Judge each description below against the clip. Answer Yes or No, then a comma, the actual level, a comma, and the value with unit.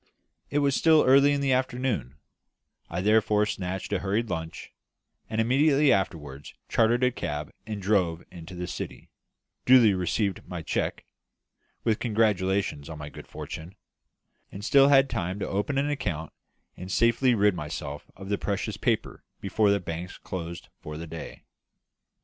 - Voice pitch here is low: Yes, low, 100 Hz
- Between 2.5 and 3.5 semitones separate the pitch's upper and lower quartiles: No, wide, 5.6 semitones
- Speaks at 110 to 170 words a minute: Yes, average, 155 wpm